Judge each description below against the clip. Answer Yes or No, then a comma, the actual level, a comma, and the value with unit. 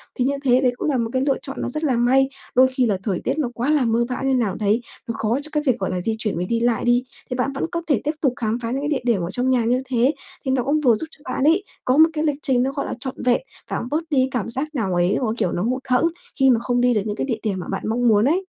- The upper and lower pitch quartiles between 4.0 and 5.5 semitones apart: No, average, 3.0 semitones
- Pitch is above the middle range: Yes, very high, 250 Hz